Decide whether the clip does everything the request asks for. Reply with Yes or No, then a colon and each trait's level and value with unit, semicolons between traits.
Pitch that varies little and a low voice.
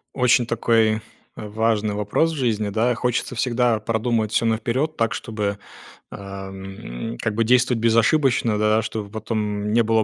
Yes: narrow, 2.0 semitones; low, 110 Hz